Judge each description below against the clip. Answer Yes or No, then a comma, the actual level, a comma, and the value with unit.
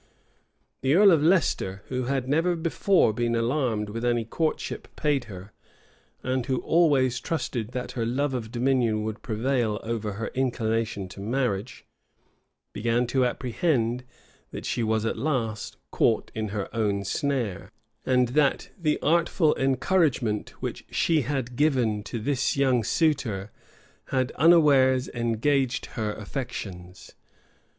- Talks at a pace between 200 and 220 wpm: No, slow, 135 wpm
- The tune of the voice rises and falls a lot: No, average, 4.0 semitones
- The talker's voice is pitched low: Yes, low, 125 Hz